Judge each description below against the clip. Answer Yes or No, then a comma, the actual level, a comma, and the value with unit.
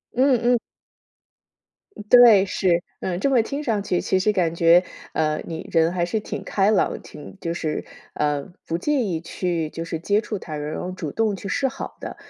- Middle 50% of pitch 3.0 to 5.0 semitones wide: Yes, average, 4.7 semitones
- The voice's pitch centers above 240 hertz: No, medium, 185 Hz